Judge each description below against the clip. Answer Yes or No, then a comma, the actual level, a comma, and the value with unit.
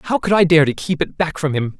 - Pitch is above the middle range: No, medium, 160 Hz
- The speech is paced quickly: Yes, fast, 335 wpm